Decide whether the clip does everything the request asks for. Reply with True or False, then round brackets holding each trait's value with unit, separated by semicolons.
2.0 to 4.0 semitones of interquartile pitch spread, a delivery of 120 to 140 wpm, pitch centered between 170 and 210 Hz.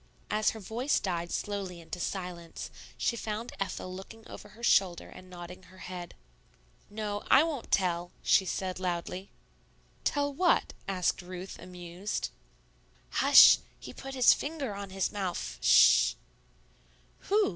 True (3.6 semitones; 135 wpm; 190 Hz)